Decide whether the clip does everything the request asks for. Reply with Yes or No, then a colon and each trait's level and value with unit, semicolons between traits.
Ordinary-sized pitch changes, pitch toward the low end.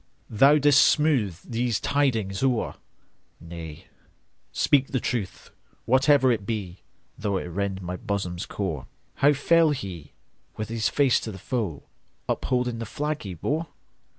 No: wide, 6.1 semitones; low, 115 Hz